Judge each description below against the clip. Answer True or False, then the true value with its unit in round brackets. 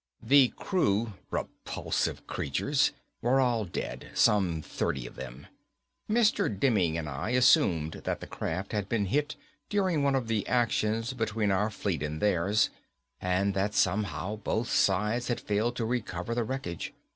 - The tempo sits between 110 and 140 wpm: False (150 wpm)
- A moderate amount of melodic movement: True (4.7 semitones)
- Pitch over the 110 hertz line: False (105 Hz)